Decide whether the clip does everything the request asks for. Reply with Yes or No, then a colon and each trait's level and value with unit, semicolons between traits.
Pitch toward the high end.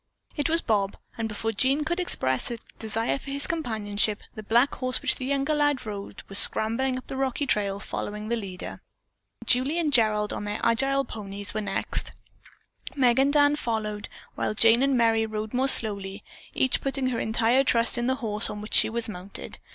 Yes: high, 230 Hz